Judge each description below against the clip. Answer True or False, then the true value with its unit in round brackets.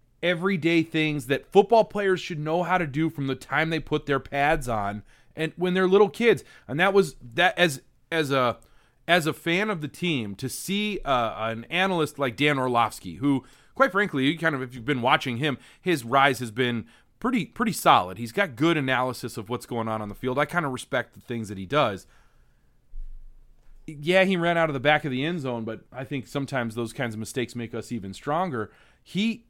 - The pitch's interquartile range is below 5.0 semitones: False (5.6 semitones)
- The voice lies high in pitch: False (140 Hz)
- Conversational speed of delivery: False (215 wpm)